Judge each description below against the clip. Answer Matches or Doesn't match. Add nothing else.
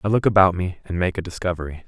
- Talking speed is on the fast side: Matches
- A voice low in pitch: Matches